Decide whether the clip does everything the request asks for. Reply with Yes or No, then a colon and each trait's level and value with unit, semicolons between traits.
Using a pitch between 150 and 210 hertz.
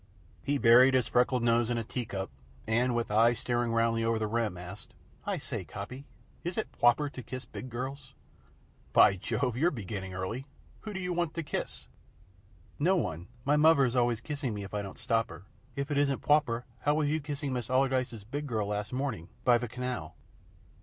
No: low, 120 Hz